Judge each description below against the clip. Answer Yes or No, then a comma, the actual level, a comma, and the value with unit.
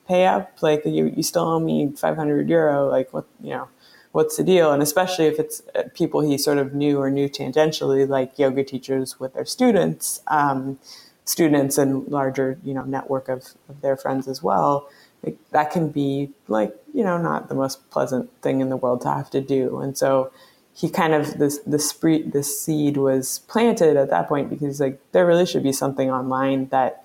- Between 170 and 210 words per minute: Yes, fast, 205 wpm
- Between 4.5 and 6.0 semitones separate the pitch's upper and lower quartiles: No, average, 2.8 semitones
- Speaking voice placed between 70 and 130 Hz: No, medium, 140 Hz